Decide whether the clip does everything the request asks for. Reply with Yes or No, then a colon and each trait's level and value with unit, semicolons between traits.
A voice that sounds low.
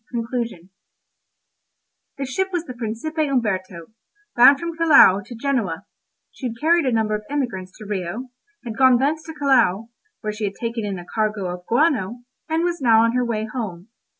No: high, 235 Hz